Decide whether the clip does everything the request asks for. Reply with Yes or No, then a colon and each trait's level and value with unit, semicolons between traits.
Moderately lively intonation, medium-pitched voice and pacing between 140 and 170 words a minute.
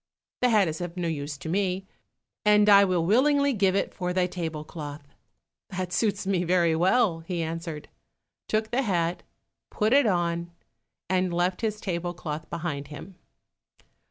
Yes: average, 3.4 semitones; medium, 180 Hz; average, 160 wpm